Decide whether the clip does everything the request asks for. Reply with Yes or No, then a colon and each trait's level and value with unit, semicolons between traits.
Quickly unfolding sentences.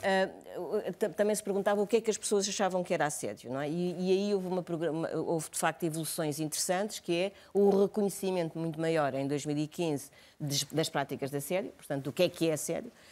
Yes: fast, 200 wpm